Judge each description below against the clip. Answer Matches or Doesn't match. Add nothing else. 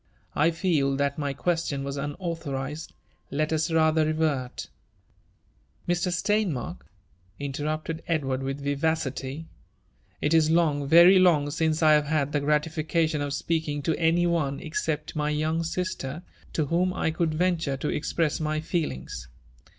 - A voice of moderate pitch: Matches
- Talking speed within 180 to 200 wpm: Doesn't match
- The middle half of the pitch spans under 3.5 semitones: Matches